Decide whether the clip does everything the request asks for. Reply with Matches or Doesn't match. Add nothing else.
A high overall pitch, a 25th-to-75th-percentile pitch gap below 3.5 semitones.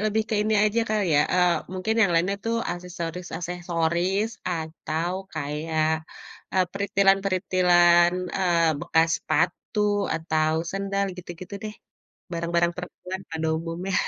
Doesn't match